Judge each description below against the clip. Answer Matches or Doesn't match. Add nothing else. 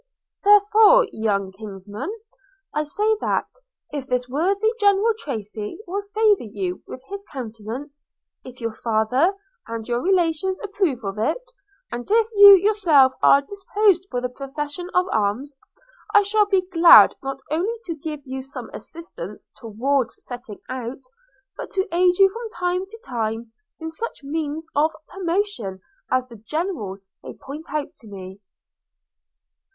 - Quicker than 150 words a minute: Doesn't match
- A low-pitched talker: Doesn't match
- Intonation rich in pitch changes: Matches